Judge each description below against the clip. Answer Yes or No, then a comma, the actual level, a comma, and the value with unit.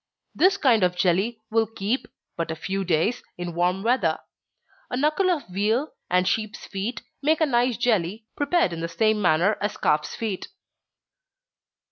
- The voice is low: No, high, 215 Hz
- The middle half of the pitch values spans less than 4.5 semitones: No, wide, 5.4 semitones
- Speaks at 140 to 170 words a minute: Yes, average, 160 wpm